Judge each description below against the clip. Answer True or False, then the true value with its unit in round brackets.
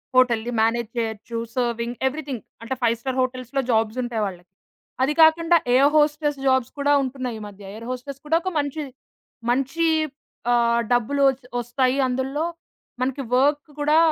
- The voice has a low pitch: False (255 Hz)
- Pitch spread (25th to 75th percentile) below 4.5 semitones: True (3.4 semitones)